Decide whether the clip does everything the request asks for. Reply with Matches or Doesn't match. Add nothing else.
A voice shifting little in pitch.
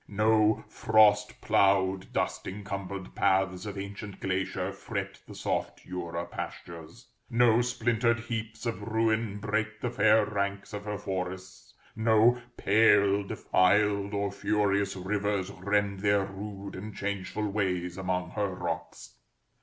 Matches